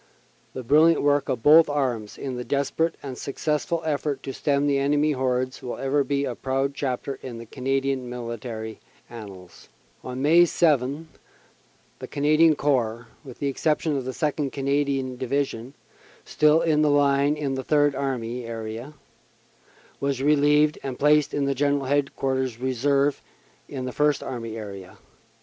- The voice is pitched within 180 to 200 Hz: No, medium, 140 Hz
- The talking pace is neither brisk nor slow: Yes, average, 150 wpm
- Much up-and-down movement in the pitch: No, narrow, 2.5 semitones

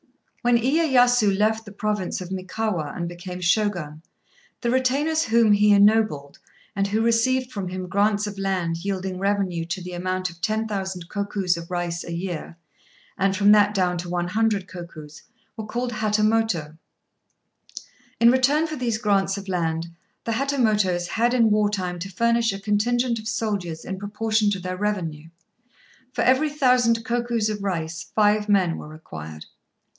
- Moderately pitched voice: No, high, 205 Hz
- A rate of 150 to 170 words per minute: Yes, average, 160 wpm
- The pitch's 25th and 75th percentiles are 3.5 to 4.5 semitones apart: Yes, average, 3.9 semitones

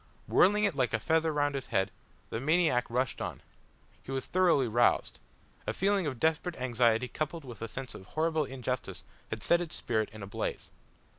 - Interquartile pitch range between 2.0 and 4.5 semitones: No, average, 5.3 semitones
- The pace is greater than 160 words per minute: Yes, average, 190 wpm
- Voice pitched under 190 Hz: Yes, low, 135 Hz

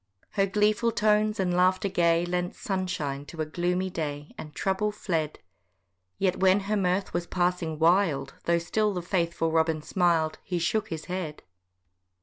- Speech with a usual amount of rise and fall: Yes, average, 3.0 semitones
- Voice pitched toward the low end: No, medium, 180 Hz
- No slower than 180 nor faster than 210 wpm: No, average, 155 wpm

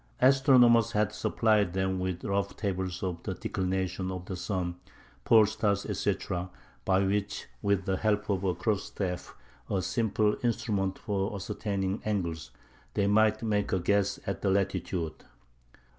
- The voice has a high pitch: No, low, 100 Hz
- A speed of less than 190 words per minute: Yes, average, 140 wpm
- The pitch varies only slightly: Yes, narrow, 2.3 semitones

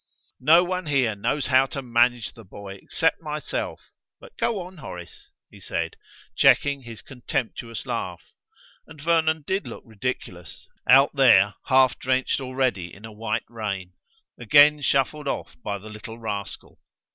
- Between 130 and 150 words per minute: Yes, average, 145 wpm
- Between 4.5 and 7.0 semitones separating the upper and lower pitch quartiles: Yes, average, 5.2 semitones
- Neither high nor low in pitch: No, low, 125 Hz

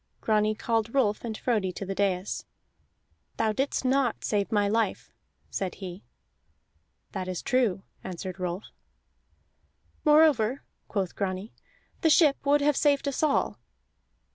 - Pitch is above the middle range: Yes, high, 215 Hz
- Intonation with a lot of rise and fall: Yes, wide, 5.9 semitones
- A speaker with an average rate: No, slow, 130 wpm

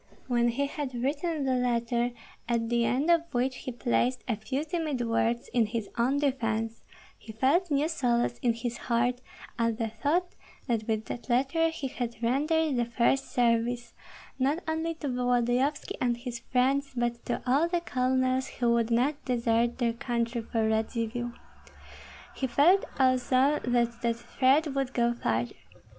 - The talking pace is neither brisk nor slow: Yes, average, 160 wpm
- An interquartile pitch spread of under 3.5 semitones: Yes, average, 2.8 semitones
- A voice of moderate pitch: No, high, 245 Hz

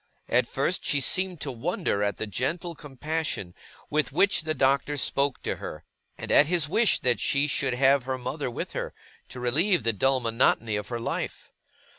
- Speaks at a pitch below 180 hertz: Yes, low, 135 Hz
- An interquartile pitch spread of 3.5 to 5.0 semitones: Yes, average, 4.1 semitones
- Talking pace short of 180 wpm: No, average, 185 wpm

